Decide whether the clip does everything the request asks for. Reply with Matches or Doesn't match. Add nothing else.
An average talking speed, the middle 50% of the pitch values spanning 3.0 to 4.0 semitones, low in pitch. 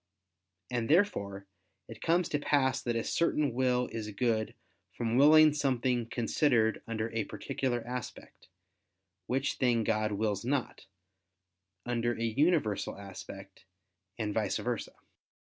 Doesn't match